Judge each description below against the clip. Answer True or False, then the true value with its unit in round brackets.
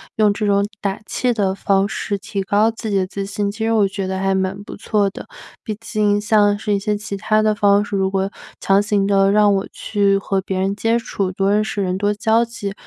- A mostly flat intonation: True (1.4 semitones)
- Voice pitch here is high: True (205 Hz)